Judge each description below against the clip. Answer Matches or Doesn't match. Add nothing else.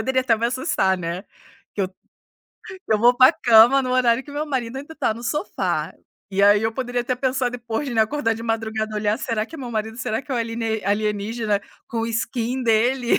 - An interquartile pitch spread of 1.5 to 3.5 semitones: Matches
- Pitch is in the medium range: Doesn't match